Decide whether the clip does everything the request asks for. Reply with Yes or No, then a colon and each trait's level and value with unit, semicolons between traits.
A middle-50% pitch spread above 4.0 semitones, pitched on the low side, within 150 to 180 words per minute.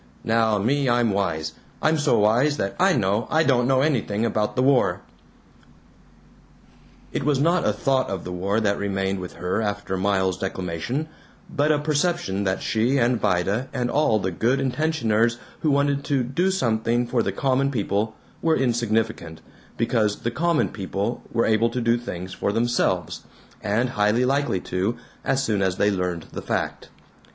Yes: average, 5.2 semitones; low, 115 Hz; average, 170 wpm